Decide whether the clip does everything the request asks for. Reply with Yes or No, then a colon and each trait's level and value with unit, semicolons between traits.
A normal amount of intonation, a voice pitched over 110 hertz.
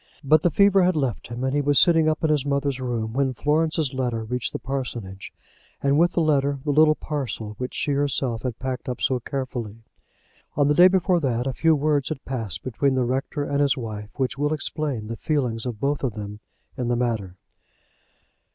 Yes: average, 3.5 semitones; low, 135 Hz